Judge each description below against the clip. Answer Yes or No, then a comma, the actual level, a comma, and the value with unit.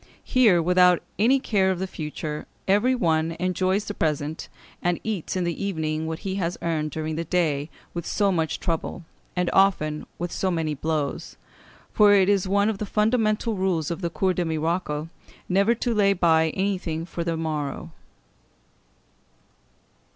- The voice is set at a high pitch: No, medium, 175 Hz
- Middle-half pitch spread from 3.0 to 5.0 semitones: Yes, average, 3.6 semitones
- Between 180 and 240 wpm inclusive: No, average, 165 wpm